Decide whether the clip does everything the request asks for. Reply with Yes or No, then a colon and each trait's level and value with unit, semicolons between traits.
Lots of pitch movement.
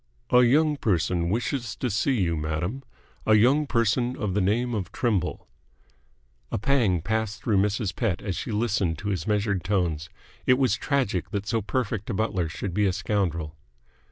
No: average, 4.6 semitones